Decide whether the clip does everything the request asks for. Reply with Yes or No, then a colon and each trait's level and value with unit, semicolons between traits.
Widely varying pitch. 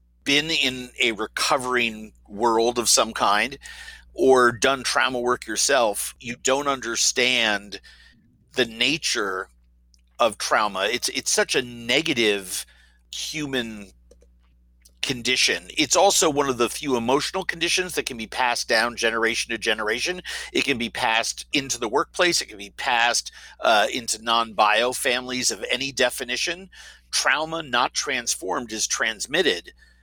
No: average, 3.9 semitones